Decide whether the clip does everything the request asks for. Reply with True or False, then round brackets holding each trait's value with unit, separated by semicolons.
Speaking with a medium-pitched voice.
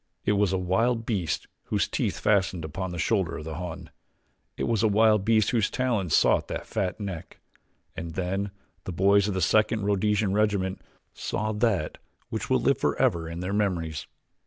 False (100 Hz)